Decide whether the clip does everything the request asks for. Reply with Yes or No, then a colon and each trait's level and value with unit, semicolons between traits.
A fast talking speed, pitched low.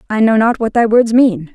No: fast, 270 wpm; high, 230 Hz